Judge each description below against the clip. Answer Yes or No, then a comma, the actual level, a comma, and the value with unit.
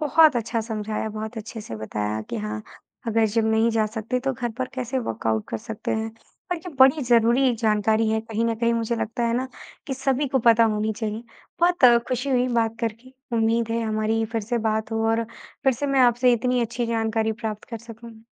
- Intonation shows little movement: Yes, narrow, 2.1 semitones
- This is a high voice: Yes, high, 230 Hz